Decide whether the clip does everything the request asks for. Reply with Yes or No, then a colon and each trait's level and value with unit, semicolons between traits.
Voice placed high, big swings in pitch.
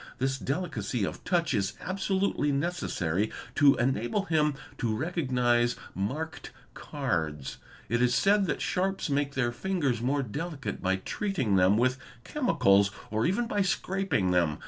No: low, 135 Hz; wide, 8.4 semitones